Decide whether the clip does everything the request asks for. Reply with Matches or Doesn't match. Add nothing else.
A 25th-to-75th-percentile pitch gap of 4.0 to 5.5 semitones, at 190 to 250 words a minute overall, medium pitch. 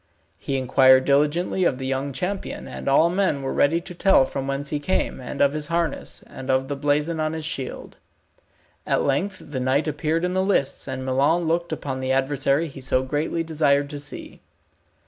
Doesn't match